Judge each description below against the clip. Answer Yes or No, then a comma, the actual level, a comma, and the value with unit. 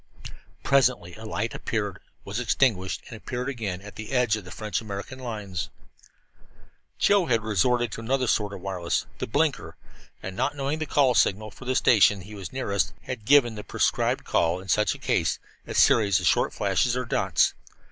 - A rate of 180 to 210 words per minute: Yes, average, 185 wpm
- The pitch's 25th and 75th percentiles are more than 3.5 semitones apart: Yes, average, 4.2 semitones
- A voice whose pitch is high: No, low, 110 Hz